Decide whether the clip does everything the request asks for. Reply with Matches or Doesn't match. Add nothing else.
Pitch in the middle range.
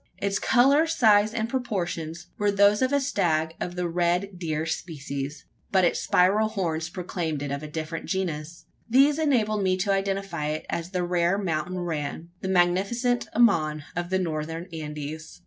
Matches